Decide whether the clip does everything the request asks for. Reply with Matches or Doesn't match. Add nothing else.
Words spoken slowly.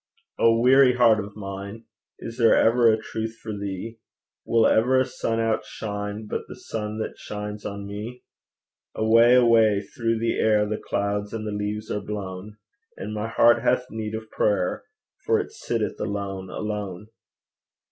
Doesn't match